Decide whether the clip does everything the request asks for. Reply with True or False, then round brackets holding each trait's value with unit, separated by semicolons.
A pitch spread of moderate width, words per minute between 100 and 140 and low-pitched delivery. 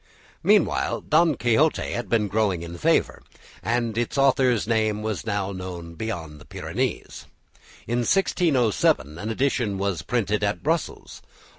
True (4.2 semitones; 135 wpm; 110 Hz)